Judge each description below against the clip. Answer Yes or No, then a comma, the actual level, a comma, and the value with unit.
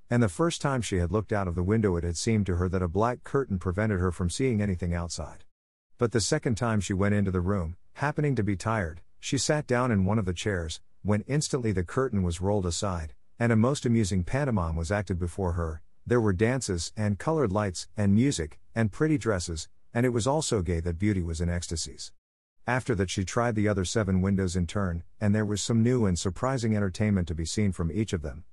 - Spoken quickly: Yes, fast, 230 wpm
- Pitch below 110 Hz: Yes, low, 100 Hz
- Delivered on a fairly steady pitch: No, average, 4.5 semitones